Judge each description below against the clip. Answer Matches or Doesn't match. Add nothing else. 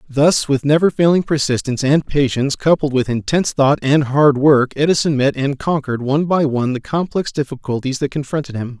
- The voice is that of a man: Matches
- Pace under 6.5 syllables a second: Matches